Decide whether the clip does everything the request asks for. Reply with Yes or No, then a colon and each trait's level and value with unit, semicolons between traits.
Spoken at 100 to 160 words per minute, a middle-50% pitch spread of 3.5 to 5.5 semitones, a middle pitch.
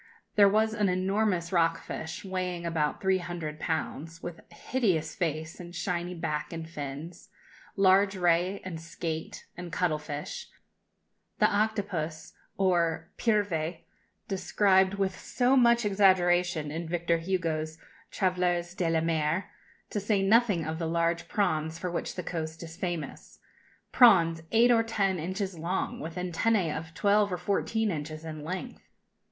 No: average, 145 wpm; average, 3.1 semitones; medium, 175 Hz